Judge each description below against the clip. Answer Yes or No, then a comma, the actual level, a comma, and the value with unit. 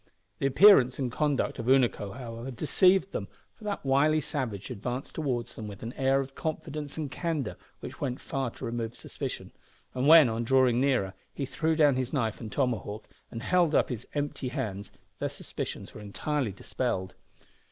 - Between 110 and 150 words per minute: No, average, 175 wpm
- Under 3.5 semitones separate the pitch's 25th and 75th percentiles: No, average, 4.1 semitones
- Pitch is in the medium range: No, low, 130 Hz